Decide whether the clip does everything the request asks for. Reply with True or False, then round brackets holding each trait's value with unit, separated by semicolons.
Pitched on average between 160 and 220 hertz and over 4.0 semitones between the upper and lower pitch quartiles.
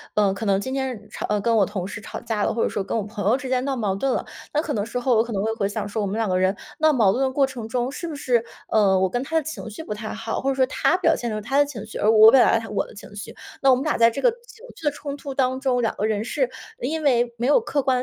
False (235 Hz; 4.4 semitones)